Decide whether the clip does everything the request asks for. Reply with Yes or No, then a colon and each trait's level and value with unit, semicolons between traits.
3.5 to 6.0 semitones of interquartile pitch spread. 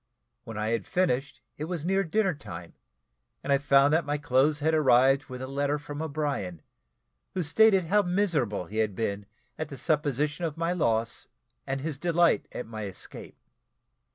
Yes: average, 4.7 semitones